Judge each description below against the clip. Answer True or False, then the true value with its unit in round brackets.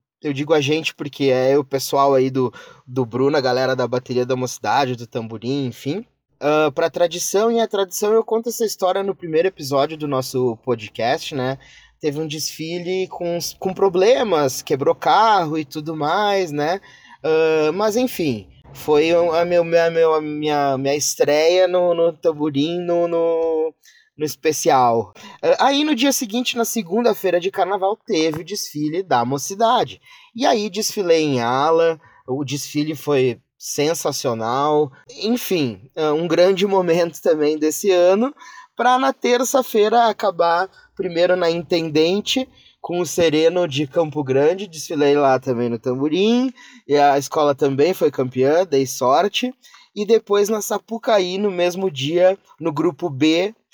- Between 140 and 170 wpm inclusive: True (150 wpm)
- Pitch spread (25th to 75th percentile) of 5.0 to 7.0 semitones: True (5.6 semitones)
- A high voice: False (165 Hz)